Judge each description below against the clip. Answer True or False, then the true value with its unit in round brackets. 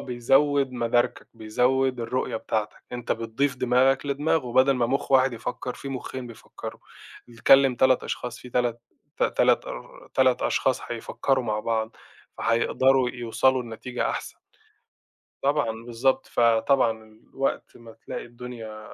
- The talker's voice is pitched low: True (125 Hz)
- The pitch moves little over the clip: True (2.3 semitones)